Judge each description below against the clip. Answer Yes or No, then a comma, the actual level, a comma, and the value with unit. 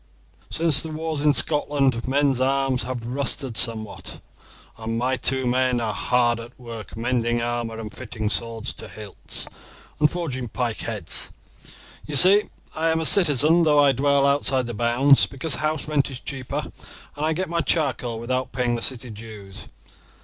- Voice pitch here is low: Yes, low, 130 Hz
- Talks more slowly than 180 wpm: Yes, average, 165 wpm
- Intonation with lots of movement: No, average, 3.6 semitones